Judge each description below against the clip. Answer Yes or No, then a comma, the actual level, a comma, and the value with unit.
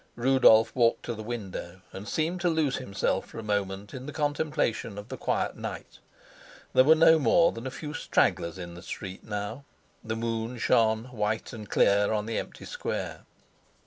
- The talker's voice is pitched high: No, low, 115 Hz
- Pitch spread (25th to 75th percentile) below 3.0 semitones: No, average, 4.7 semitones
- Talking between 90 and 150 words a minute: No, average, 180 wpm